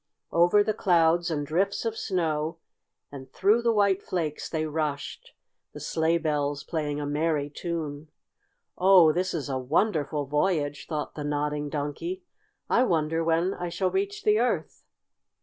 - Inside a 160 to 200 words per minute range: No, average, 150 wpm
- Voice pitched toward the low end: No, medium, 160 Hz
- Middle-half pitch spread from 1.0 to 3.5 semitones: No, average, 4.0 semitones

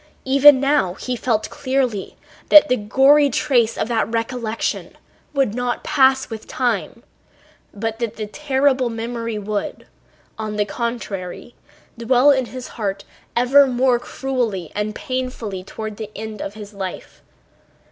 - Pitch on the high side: Yes, high, 235 Hz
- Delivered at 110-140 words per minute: Yes, slow, 135 wpm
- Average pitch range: Yes, average, 3.6 semitones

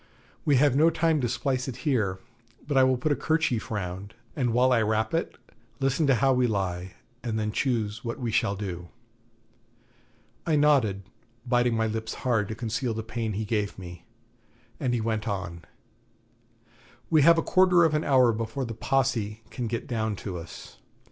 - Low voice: Yes, low, 115 Hz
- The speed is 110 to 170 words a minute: No, average, 180 wpm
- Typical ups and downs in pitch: Yes, average, 4.1 semitones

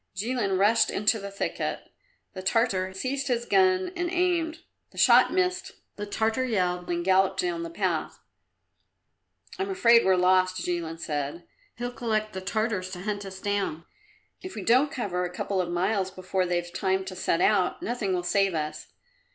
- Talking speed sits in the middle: Yes, average, 170 wpm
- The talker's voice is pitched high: Yes, high, 200 Hz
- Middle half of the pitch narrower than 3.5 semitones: No, average, 4.8 semitones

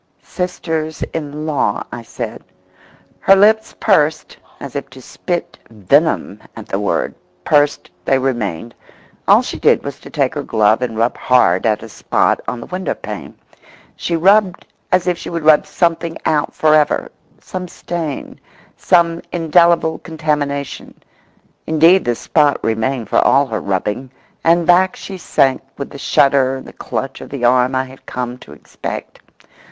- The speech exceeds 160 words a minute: No, average, 155 wpm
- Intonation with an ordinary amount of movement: Yes, average, 5.0 semitones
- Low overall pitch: No, medium, 145 Hz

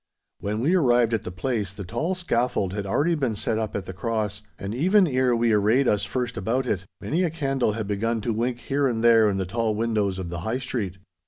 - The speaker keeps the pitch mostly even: No, average, 3.9 semitones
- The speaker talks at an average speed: No, fast, 235 wpm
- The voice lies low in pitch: Yes, low, 115 Hz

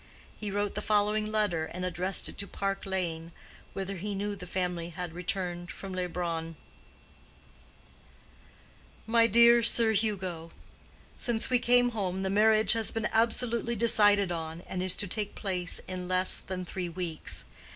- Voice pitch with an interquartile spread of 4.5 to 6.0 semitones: No, average, 3.2 semitones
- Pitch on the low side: No, high, 195 Hz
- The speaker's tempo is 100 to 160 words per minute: Yes, average, 150 wpm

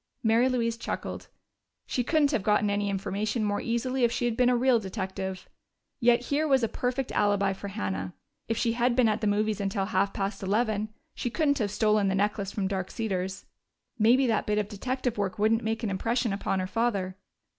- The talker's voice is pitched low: No, high, 215 Hz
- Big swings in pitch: No, average, 3.3 semitones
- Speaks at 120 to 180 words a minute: No, average, 200 wpm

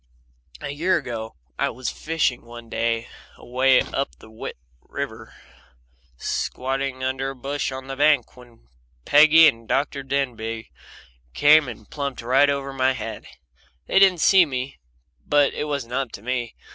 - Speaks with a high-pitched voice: No, low, 135 Hz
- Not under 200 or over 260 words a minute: No, average, 145 wpm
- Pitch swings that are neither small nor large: Yes, average, 3.0 semitones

